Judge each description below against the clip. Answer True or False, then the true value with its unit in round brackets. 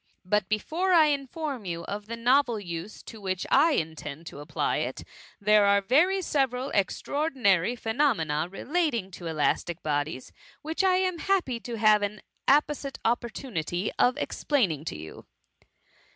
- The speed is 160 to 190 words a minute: False (150 wpm)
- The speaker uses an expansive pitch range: True (7.9 semitones)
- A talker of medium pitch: False (215 Hz)